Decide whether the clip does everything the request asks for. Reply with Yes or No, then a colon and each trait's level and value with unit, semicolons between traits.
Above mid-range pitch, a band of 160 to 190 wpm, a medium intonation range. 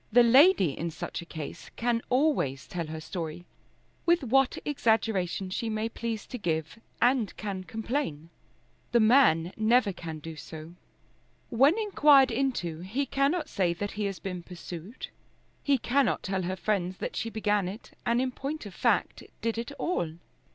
No: high, 215 Hz; average, 165 wpm; wide, 6.5 semitones